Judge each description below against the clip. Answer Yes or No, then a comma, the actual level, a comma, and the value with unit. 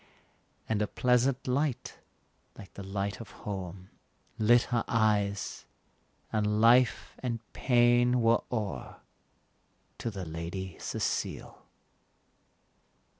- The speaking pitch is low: Yes, low, 110 Hz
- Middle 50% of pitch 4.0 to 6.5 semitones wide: No, average, 3.4 semitones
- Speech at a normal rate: No, slow, 100 wpm